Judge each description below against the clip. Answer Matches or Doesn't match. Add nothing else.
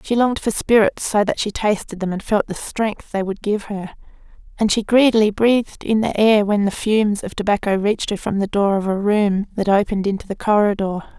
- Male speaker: Doesn't match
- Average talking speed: Doesn't match